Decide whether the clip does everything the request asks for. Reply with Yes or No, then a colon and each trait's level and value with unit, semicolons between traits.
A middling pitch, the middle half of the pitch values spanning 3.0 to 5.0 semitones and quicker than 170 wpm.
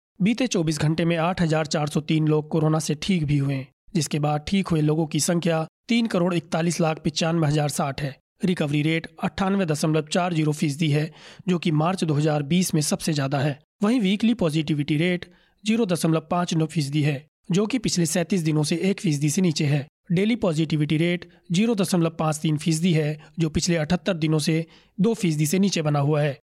No: medium, 165 Hz; narrow, 2.6 semitones; average, 180 wpm